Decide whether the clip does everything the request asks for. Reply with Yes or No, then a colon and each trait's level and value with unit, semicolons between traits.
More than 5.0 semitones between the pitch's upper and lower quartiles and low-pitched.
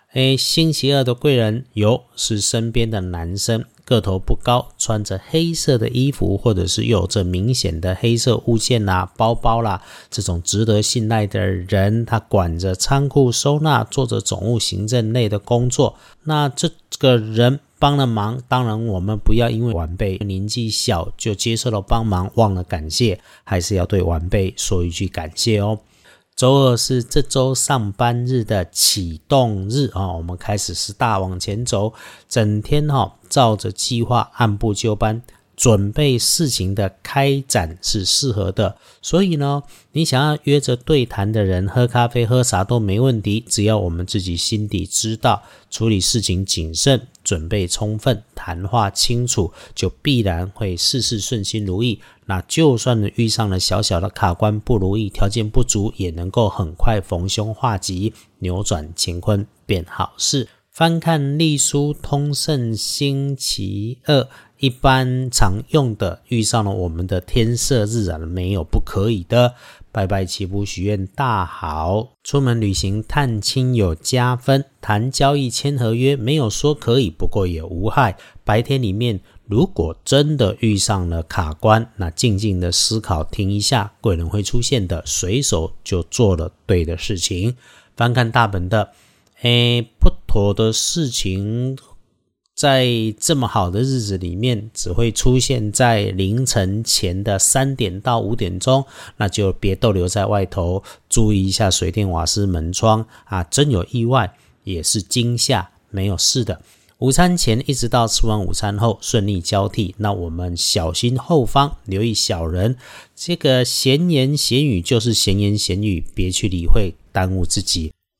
No: average, 4.3 semitones; low, 110 Hz